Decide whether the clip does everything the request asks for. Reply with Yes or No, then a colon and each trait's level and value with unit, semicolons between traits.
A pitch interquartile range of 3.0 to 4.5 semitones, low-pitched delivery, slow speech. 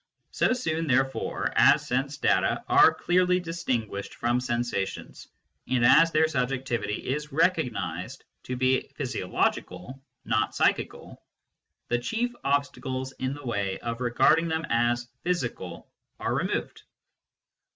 No: average, 4.9 semitones; low, 130 Hz; slow, 130 wpm